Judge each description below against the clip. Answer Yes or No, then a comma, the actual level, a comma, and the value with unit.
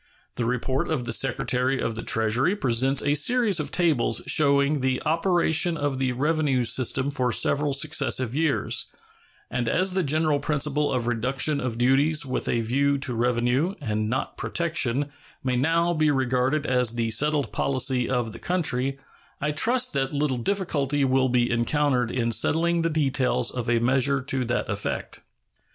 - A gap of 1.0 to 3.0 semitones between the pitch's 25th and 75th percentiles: No, average, 3.5 semitones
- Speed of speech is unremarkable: Yes, average, 165 wpm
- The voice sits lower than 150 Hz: Yes, low, 135 Hz